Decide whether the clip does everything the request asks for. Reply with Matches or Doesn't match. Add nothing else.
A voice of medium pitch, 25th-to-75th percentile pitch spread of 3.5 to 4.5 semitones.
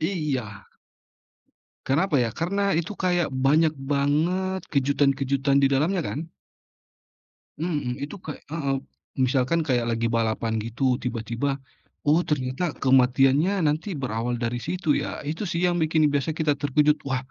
Matches